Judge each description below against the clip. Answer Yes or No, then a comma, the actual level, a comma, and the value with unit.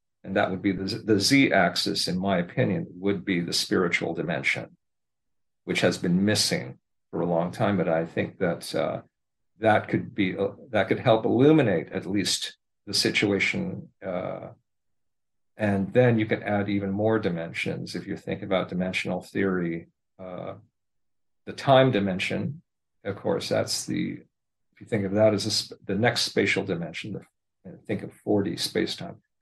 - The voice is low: Yes, low, 100 Hz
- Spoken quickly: No, average, 160 wpm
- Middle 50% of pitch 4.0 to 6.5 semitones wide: No, narrow, 2.6 semitones